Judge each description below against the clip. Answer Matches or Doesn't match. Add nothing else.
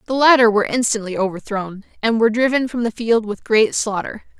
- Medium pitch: Doesn't match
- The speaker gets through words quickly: Doesn't match